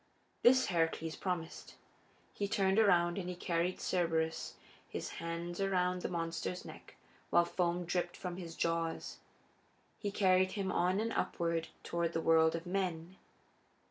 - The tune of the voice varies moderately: No, narrow, 2.0 semitones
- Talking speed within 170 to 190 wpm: No, average, 140 wpm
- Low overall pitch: No, medium, 175 Hz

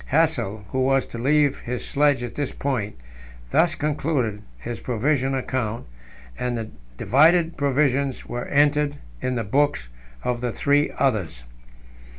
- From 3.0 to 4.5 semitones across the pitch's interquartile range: Yes, average, 3.5 semitones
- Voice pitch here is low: Yes, low, 130 Hz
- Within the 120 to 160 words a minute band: Yes, average, 140 wpm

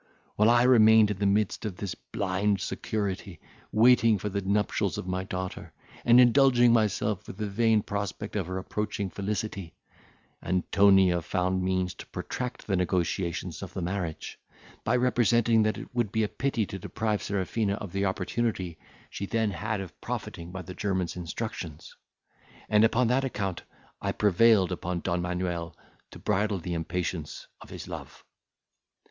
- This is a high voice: No, low, 100 Hz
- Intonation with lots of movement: No, average, 3.2 semitones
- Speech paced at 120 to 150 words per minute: No, average, 160 wpm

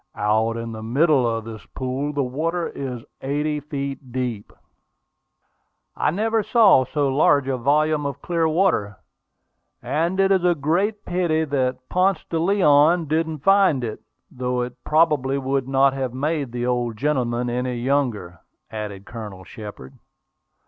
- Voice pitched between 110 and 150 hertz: Yes, low, 135 Hz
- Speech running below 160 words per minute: Yes, average, 150 wpm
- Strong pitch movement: No, average, 4.5 semitones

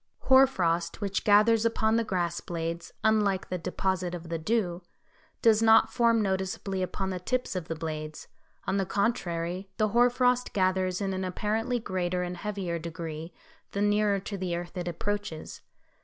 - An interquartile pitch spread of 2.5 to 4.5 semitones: Yes, average, 3.6 semitones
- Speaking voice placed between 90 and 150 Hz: No, high, 190 Hz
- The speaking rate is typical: Yes, average, 170 wpm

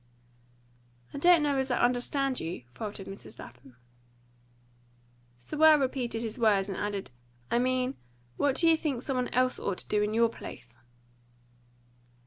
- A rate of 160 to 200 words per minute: No, average, 150 wpm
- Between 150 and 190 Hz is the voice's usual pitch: No, high, 245 Hz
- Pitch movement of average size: Yes, average, 4.8 semitones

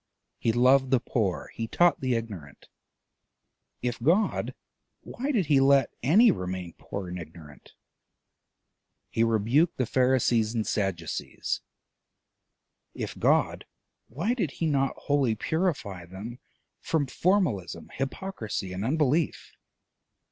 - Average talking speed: No, slow, 115 wpm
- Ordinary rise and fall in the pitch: No, wide, 7.0 semitones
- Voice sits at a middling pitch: No, low, 125 Hz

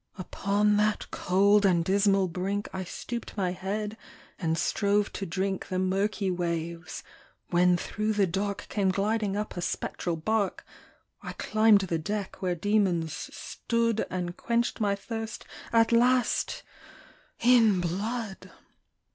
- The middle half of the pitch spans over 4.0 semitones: No, average, 2.8 semitones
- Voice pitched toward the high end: Yes, high, 200 Hz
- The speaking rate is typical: No, slow, 130 wpm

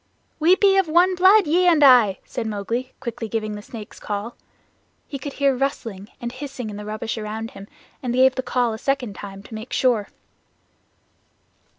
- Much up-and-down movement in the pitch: No, average, 4.5 semitones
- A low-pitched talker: No, high, 245 Hz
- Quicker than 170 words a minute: Yes, average, 190 wpm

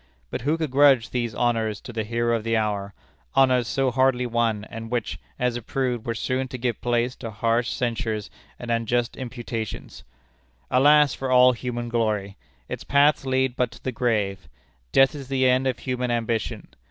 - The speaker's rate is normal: Yes, average, 180 wpm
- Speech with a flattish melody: Yes, narrow, 2.2 semitones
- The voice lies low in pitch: Yes, low, 120 Hz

